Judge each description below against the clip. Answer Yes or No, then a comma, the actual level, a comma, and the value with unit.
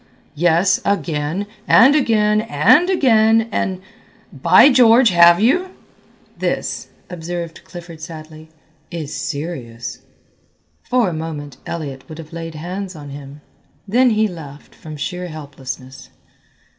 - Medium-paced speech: No, slow, 120 wpm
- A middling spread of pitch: No, wide, 5.8 semitones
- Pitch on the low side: No, medium, 170 Hz